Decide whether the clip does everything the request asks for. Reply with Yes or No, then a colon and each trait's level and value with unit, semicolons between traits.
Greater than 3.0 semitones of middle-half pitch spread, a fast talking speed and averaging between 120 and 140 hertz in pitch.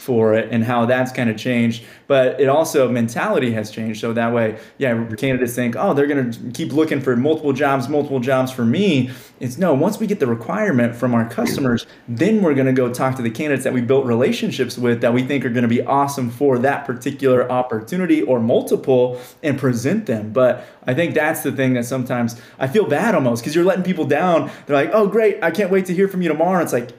Yes: average, 3.4 semitones; fast, 225 wpm; low, 130 Hz